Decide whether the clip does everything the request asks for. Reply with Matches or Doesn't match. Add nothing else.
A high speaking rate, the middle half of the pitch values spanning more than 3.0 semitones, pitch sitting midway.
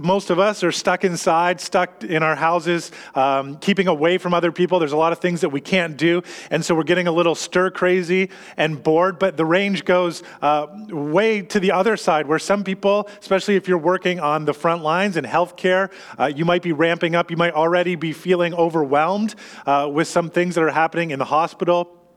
Doesn't match